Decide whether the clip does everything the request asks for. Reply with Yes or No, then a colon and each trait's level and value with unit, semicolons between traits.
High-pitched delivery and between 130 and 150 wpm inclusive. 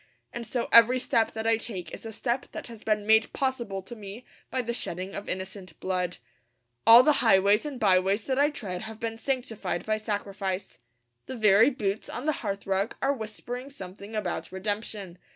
No: high, 215 Hz; average, 185 wpm